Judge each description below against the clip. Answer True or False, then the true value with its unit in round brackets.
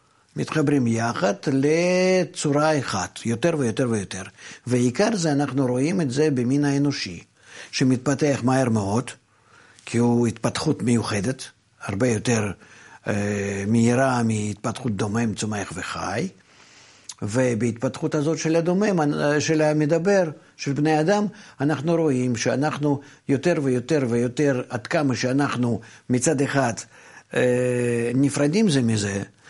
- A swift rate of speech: False (110 wpm)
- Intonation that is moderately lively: True (4.6 semitones)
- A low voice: True (130 Hz)